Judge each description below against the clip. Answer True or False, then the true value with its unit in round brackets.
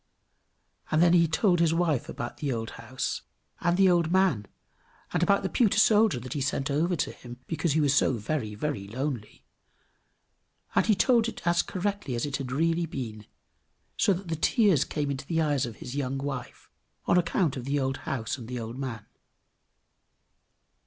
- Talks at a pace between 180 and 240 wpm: True (185 wpm)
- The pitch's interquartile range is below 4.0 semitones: False (5.3 semitones)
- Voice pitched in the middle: True (145 Hz)